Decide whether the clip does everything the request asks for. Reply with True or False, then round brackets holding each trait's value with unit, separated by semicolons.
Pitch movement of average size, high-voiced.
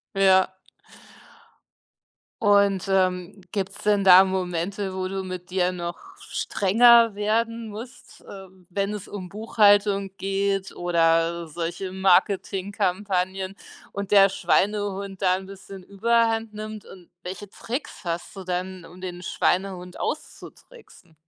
False (1.9 semitones; 195 Hz)